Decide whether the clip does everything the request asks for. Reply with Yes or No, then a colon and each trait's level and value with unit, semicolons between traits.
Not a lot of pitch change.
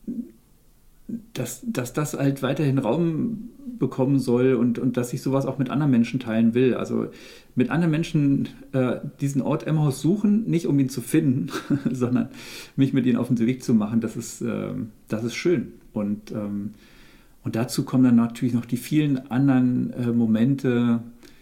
No: average, 3.6 semitones